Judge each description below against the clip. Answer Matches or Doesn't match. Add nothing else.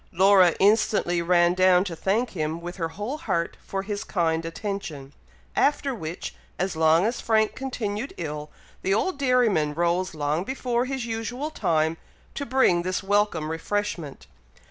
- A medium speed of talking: Matches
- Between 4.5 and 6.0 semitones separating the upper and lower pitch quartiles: Matches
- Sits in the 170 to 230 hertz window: Matches